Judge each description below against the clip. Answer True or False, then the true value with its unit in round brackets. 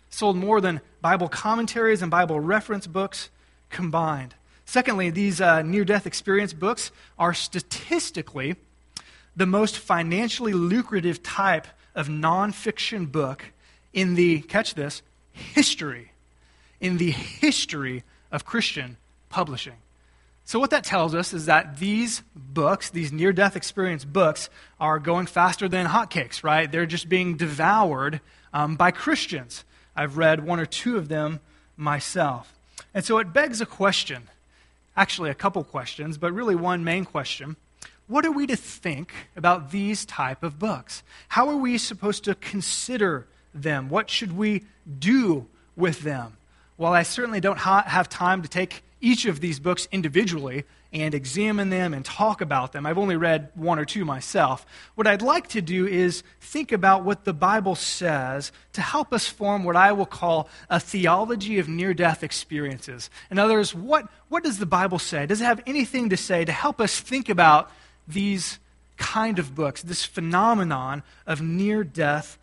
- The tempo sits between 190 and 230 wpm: False (155 wpm)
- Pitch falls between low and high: True (180 Hz)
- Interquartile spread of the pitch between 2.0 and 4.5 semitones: False (4.9 semitones)